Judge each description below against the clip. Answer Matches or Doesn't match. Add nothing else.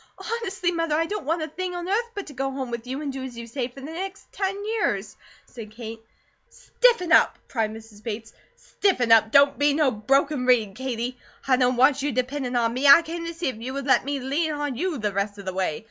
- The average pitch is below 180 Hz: Doesn't match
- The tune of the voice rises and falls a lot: Matches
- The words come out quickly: Matches